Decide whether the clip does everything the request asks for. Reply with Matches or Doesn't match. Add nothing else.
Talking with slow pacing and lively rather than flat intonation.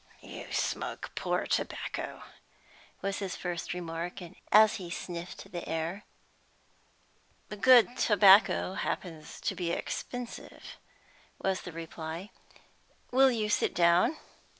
Doesn't match